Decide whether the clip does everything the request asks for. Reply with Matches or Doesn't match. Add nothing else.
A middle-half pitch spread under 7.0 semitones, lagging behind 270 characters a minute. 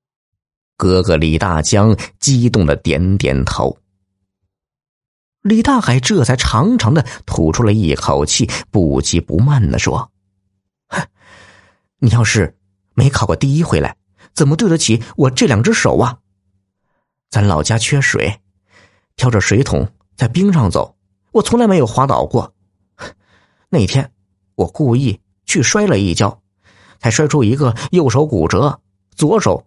Matches